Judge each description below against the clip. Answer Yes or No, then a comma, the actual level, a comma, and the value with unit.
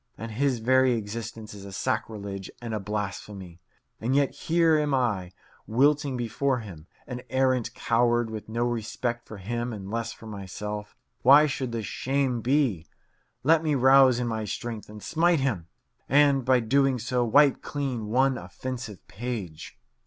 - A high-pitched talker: No, low, 120 Hz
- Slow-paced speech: No, average, 160 wpm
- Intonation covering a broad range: No, average, 4.0 semitones